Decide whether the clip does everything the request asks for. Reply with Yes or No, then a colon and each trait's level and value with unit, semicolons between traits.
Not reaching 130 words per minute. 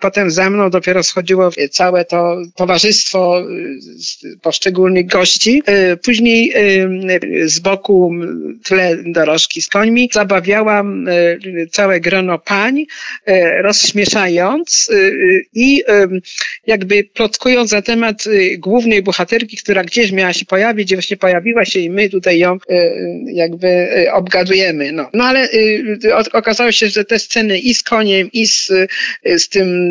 Yes: average, 120 wpm